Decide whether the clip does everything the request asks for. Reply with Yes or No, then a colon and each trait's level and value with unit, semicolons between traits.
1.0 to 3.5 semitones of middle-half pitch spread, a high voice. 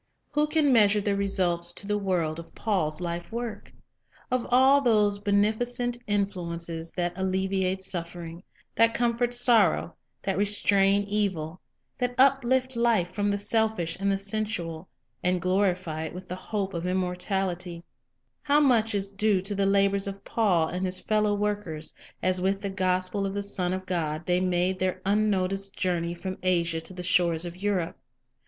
Yes: average, 2.8 semitones; high, 195 Hz